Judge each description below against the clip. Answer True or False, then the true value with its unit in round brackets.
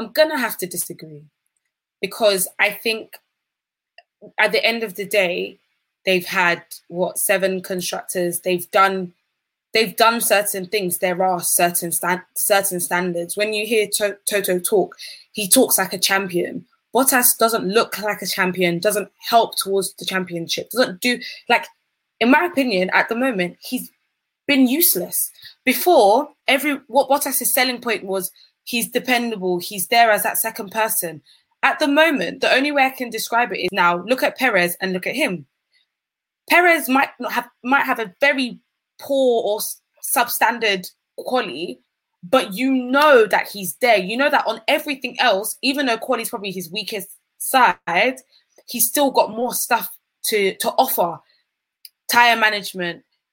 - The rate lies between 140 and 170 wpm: True (160 wpm)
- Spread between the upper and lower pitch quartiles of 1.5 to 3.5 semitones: False (5.2 semitones)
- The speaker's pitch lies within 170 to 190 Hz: False (220 Hz)